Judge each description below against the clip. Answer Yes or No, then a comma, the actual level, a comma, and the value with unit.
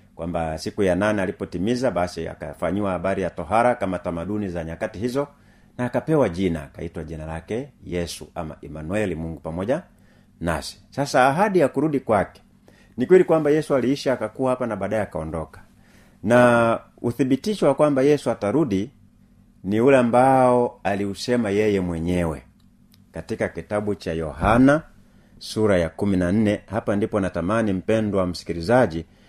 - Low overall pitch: Yes, low, 105 Hz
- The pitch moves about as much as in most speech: No, wide, 5.8 semitones